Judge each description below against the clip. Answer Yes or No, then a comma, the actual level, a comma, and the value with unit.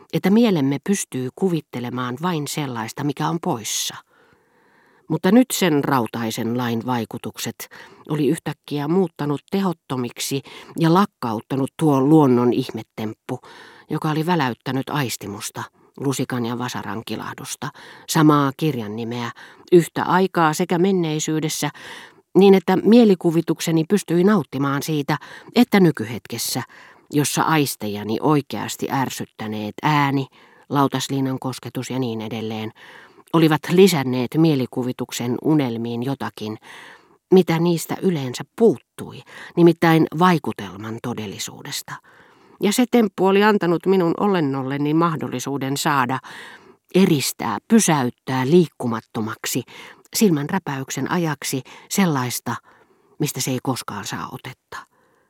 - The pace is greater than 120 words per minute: No, average, 100 wpm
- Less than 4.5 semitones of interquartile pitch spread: No, wide, 5.4 semitones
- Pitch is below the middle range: No, medium, 145 Hz